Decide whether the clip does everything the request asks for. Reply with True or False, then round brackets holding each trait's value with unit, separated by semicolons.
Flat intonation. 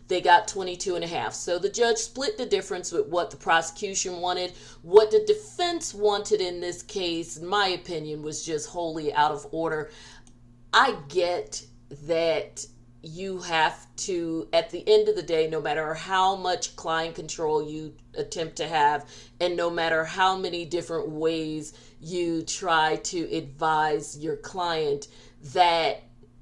False (3.5 semitones)